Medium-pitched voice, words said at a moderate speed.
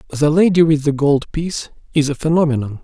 Yes: medium, 150 Hz; average, 190 wpm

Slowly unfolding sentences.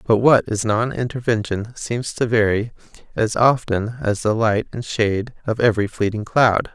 No: average, 170 wpm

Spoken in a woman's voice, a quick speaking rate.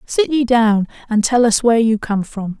Yes: female; fast, 230 wpm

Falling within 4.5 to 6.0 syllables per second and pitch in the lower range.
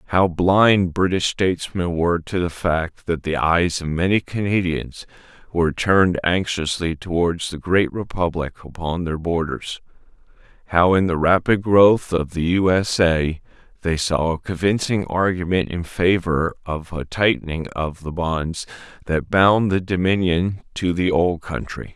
No: 4.3 syllables/s; very low, 85 Hz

